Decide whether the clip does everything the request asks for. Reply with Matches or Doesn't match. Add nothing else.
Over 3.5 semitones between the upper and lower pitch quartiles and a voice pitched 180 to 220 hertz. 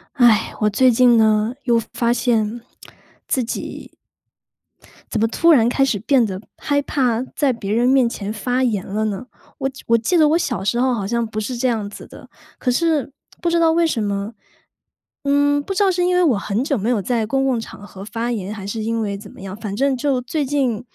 Doesn't match